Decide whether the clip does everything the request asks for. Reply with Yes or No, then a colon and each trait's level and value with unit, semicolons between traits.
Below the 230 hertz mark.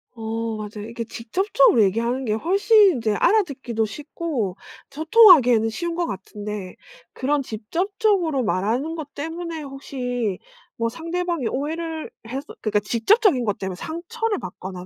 No: very high, 265 Hz